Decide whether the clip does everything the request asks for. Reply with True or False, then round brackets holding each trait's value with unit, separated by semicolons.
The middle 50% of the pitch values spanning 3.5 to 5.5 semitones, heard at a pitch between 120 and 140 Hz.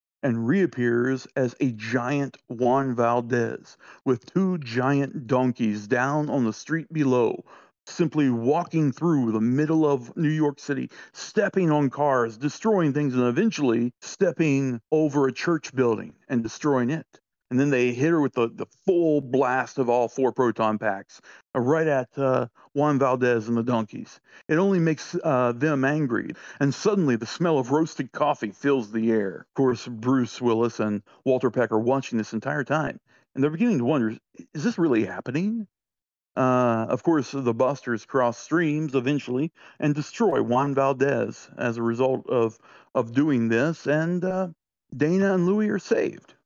True (4.0 semitones; 135 Hz)